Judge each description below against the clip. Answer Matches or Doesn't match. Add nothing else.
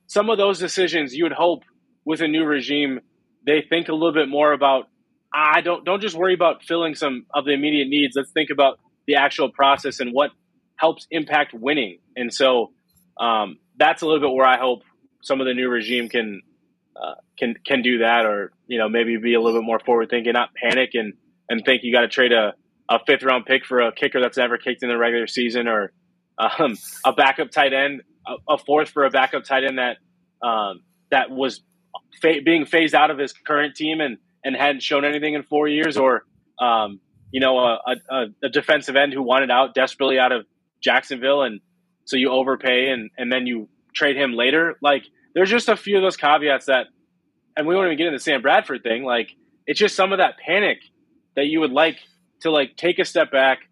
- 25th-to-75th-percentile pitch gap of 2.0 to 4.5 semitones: Matches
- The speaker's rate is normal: Doesn't match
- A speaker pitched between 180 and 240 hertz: Doesn't match